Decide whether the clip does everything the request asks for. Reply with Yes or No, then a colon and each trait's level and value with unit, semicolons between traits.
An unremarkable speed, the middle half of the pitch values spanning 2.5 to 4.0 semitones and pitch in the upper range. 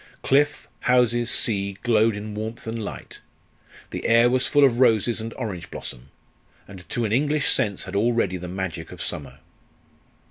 No: average, 165 wpm; average, 3.4 semitones; low, 115 Hz